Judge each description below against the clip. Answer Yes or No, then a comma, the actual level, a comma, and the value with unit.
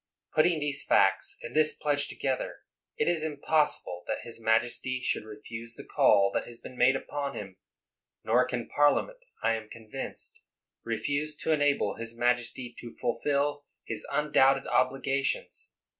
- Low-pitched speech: Yes, low, 130 Hz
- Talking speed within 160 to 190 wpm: No, average, 145 wpm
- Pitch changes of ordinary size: Yes, average, 3.9 semitones